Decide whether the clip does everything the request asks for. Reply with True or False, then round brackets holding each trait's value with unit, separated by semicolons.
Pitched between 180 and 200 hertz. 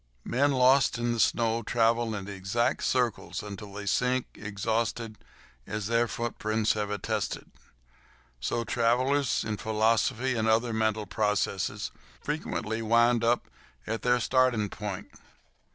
False (115 Hz)